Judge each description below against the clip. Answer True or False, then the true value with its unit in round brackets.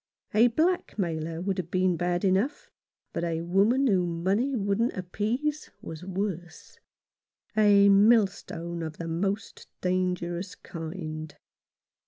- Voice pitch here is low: False (185 Hz)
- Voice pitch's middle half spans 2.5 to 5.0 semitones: True (3.5 semitones)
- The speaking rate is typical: False (120 wpm)